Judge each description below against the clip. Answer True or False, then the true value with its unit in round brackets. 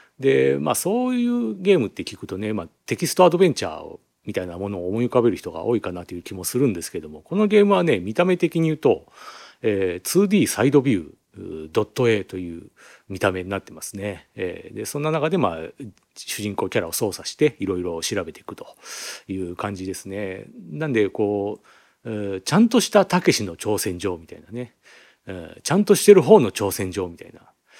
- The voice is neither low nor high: False (110 Hz)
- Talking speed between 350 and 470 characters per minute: True (370 characters per minute)